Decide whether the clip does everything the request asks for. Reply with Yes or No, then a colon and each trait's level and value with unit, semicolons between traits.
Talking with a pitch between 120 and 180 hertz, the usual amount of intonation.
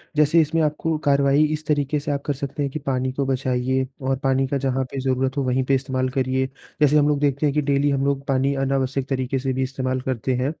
No: low, 135 Hz; narrow, 1.5 semitones